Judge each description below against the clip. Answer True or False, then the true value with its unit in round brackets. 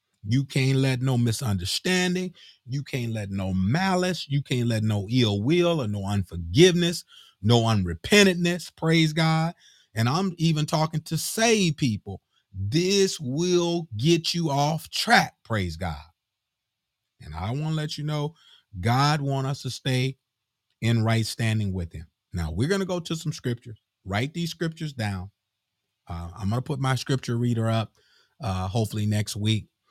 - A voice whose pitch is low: True (125 Hz)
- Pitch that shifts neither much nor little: False (7.3 semitones)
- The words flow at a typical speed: True (160 wpm)